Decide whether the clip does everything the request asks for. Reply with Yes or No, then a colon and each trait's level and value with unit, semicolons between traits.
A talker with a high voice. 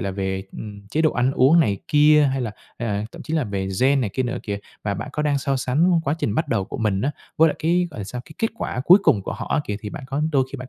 No: low, 130 Hz